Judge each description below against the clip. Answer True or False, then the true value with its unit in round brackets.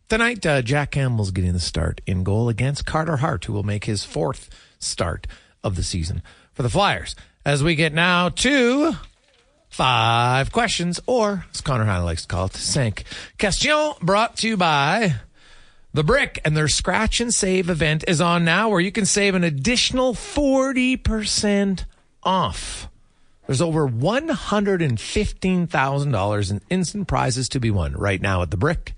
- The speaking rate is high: False (175 wpm)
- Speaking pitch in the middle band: True (155 Hz)